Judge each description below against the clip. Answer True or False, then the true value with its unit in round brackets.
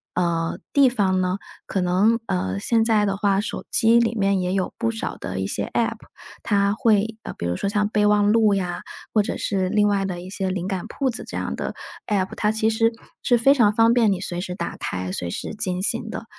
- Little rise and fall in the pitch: False (3.2 semitones)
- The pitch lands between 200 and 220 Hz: True (205 Hz)